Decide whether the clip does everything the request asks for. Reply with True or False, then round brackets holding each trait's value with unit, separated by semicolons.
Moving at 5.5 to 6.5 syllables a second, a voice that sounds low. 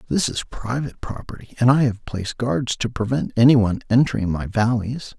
True (5.6 syllables/s; 115 Hz)